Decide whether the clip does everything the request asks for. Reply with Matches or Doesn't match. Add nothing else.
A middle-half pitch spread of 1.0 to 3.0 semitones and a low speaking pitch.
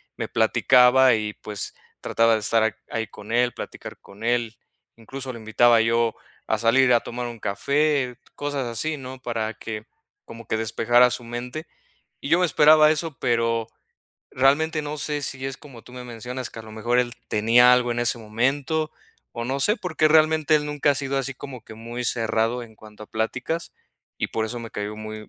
Doesn't match